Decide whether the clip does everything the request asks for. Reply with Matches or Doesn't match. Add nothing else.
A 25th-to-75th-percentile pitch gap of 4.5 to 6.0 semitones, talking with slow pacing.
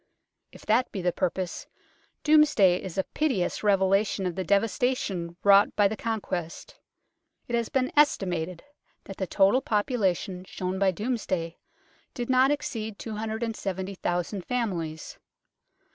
Doesn't match